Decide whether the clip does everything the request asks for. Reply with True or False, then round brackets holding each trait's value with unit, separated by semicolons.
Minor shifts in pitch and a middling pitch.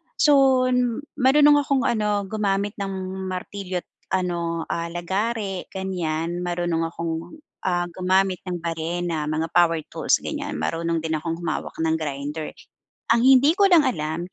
False (3.5 semitones; 180 Hz)